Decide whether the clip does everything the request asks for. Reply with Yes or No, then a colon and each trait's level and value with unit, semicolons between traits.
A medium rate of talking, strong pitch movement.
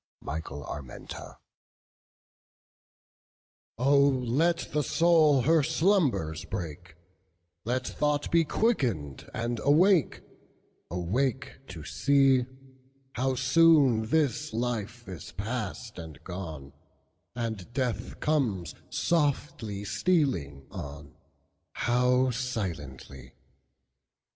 No: slow, 75 wpm; wide, 8.0 semitones